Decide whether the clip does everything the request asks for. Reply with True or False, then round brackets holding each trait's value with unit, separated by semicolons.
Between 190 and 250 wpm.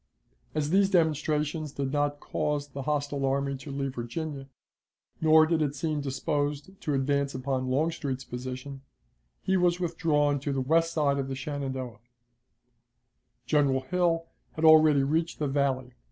False (145 wpm)